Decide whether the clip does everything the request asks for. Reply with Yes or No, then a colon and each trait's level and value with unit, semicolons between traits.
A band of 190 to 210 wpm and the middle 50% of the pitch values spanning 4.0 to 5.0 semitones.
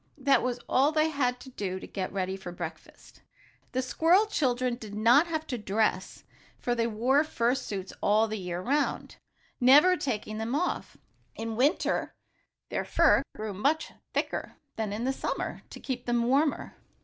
No: average, 170 wpm; average, 4.7 semitones